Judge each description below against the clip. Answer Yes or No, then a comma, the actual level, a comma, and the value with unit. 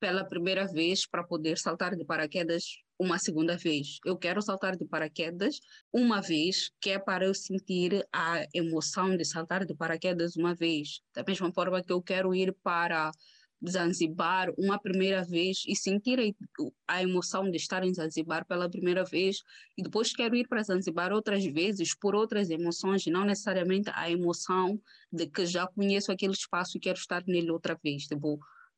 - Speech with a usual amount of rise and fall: No, narrow, 2.3 semitones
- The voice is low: No, medium, 185 Hz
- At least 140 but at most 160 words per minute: No, average, 170 wpm